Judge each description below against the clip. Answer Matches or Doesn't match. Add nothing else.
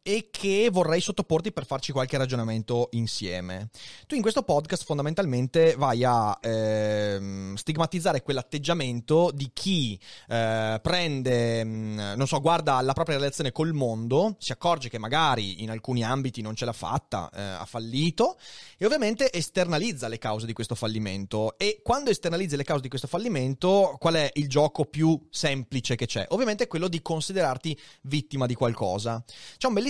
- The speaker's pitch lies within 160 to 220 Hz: Doesn't match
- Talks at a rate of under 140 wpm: Doesn't match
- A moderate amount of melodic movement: Doesn't match